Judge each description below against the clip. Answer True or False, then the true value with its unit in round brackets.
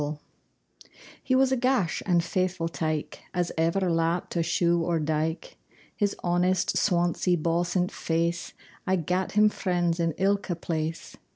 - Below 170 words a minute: True (145 wpm)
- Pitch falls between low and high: True (175 Hz)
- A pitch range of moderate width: False (2.1 semitones)